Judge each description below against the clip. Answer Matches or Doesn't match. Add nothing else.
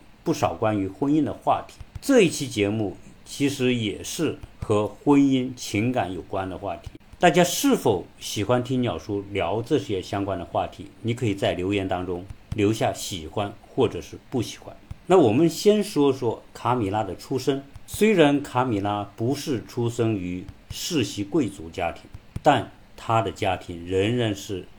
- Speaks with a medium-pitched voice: Doesn't match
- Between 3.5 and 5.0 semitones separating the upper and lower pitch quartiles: Doesn't match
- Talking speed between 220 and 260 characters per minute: Matches